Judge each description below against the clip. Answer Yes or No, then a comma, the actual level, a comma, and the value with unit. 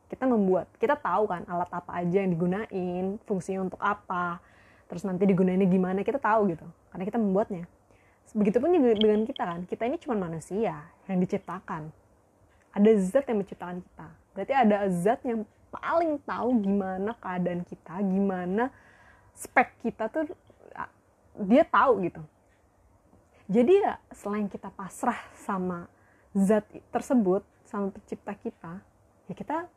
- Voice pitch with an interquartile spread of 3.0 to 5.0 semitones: Yes, average, 3.9 semitones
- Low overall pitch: No, high, 195 Hz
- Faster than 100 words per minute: Yes, average, 135 wpm